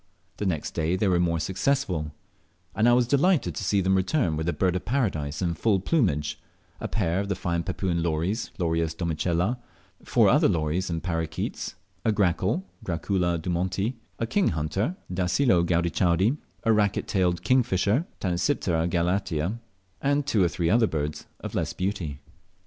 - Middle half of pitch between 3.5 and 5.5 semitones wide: Yes, average, 4.1 semitones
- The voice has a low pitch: Yes, very low, 90 Hz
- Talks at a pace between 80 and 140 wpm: No, average, 160 wpm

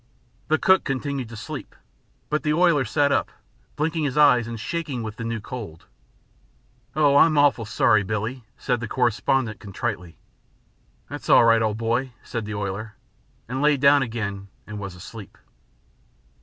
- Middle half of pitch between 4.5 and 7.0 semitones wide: Yes, average, 4.8 semitones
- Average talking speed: Yes, average, 155 wpm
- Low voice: Yes, low, 120 Hz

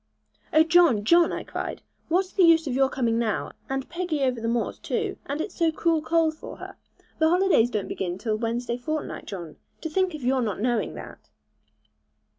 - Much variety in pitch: Yes, wide, 6.0 semitones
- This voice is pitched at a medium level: No, very high, 275 Hz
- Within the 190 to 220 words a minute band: Yes, average, 195 wpm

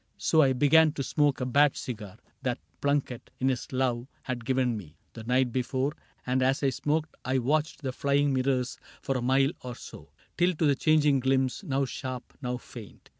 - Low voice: Yes, low, 130 Hz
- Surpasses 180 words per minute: Yes, average, 190 wpm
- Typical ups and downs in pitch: No, narrow, 2.2 semitones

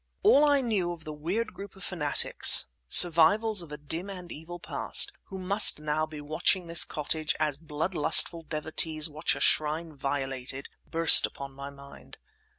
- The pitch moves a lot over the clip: No, average, 3.3 semitones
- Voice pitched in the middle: Yes, medium, 160 Hz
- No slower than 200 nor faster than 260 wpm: No, average, 155 wpm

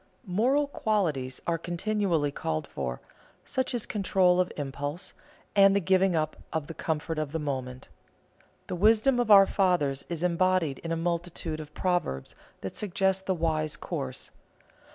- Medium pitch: Yes, medium, 170 Hz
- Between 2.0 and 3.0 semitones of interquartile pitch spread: No, average, 4.4 semitones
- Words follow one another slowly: No, average, 155 wpm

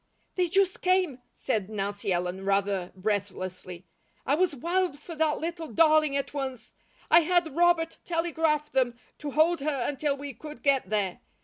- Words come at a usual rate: Yes, average, 155 wpm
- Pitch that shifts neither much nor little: No, wide, 7.7 semitones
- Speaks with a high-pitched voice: Yes, very high, 290 Hz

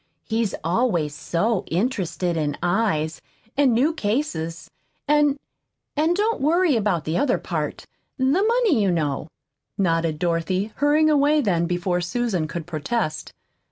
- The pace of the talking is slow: Yes, slow, 130 wpm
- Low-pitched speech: No, high, 205 Hz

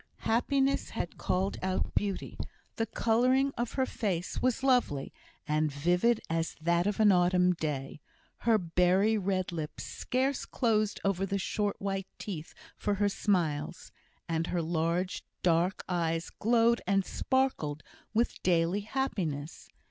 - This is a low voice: No, high, 190 Hz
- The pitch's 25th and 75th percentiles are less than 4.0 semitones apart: No, average, 5.0 semitones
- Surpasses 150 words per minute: No, slow, 135 wpm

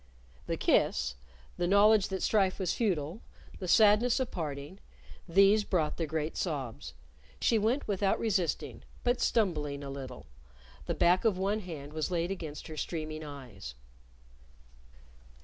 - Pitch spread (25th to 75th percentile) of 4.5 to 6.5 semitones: Yes, wide, 5.4 semitones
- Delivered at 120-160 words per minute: Yes, average, 140 wpm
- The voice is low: No, medium, 175 Hz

